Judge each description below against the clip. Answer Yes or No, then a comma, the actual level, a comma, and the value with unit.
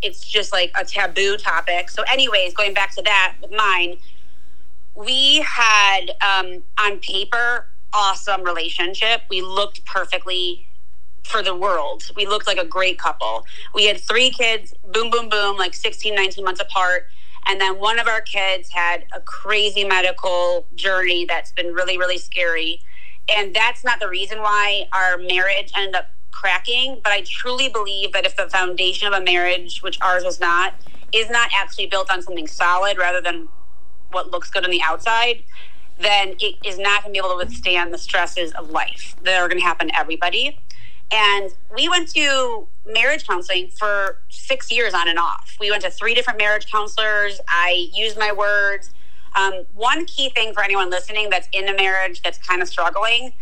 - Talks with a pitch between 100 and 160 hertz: No, high, 195 Hz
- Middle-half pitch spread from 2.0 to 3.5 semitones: Yes, average, 2.9 semitones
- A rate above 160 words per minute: Yes, average, 180 wpm